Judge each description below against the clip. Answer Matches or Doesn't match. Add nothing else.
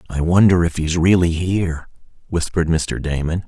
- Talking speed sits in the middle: Matches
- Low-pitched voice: Matches